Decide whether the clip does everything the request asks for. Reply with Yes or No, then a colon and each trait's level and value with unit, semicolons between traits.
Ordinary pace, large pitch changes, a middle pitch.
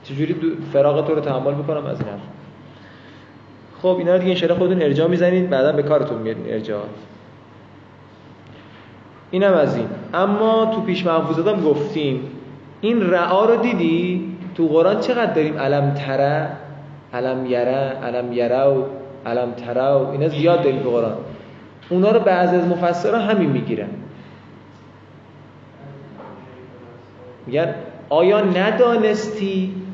Yes: average, 130 wpm; wide, 5.8 semitones; medium, 150 Hz